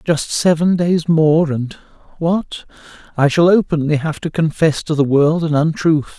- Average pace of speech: Yes, average, 155 wpm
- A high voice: No, medium, 155 Hz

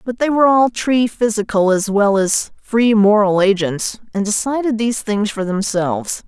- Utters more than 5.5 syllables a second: No, 4.7 syllables/s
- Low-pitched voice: No, high, 215 Hz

